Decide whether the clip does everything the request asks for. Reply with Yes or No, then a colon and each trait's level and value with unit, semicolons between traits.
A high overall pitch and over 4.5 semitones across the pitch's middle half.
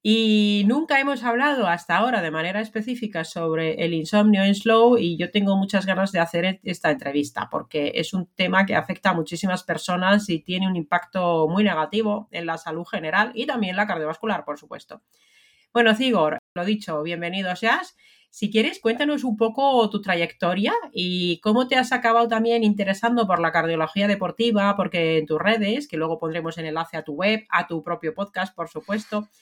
Yes: high, 195 Hz; average, 4.9 semitones